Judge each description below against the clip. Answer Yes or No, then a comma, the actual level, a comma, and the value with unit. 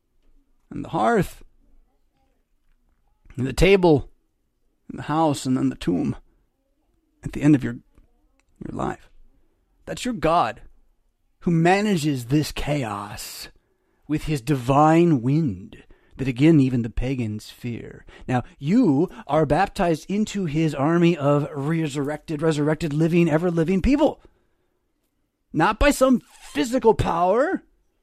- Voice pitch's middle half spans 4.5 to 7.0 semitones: No, average, 4.1 semitones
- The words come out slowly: Yes, slow, 120 wpm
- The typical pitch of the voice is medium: Yes, medium, 155 Hz